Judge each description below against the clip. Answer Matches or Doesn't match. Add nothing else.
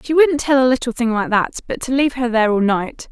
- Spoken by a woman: Matches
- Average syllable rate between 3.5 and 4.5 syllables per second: Doesn't match